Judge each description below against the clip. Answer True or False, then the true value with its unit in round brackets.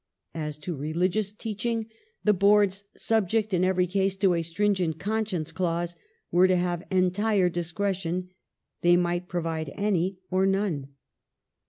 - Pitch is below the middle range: False (185 Hz)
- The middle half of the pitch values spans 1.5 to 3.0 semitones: True (2.7 semitones)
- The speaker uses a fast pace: False (145 wpm)